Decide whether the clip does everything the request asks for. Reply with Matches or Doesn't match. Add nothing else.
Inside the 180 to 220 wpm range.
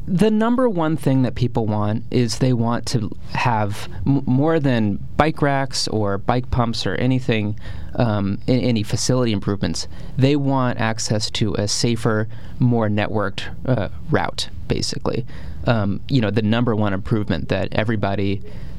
Doesn't match